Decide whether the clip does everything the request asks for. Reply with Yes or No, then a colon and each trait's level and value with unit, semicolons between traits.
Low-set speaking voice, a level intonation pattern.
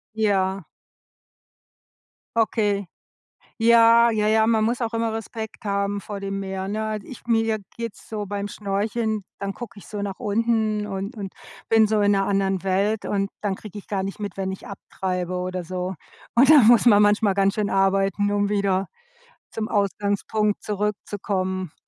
No: high, 205 Hz; narrow, 2.0 semitones